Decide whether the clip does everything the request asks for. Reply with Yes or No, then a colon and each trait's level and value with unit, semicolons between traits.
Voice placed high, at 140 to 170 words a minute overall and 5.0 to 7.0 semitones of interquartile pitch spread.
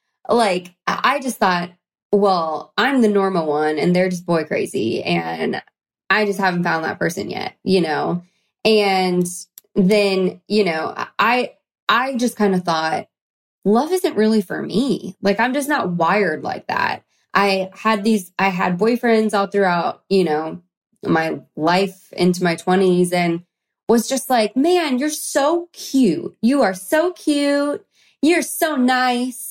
Yes: high, 200 Hz; average, 155 wpm; wide, 5.6 semitones